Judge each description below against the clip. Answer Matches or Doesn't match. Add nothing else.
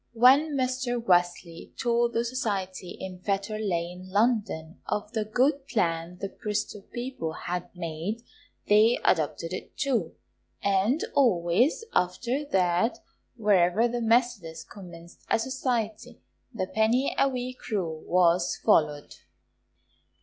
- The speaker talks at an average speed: Doesn't match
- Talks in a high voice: Matches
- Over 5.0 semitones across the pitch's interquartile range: Matches